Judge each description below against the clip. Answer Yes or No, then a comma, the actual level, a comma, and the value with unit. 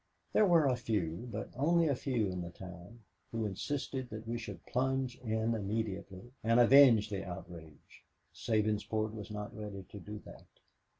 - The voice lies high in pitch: No, low, 110 Hz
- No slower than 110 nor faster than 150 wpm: No, average, 165 wpm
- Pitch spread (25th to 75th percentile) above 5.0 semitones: No, average, 3.6 semitones